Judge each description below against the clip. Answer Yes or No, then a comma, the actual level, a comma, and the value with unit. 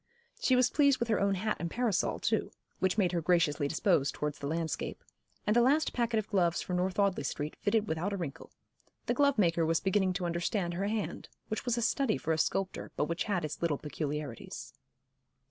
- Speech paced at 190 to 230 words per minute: Yes, fast, 205 wpm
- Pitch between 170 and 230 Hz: Yes, medium, 185 Hz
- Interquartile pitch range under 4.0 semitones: No, average, 4.8 semitones